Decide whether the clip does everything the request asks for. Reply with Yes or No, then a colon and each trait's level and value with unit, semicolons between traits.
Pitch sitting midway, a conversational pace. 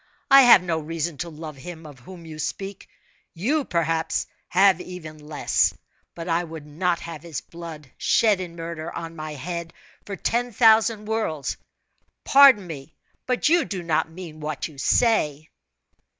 Yes: medium, 170 Hz; average, 160 wpm